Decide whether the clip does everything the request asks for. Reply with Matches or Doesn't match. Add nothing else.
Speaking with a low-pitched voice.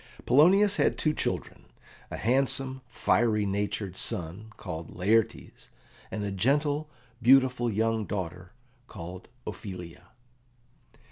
Matches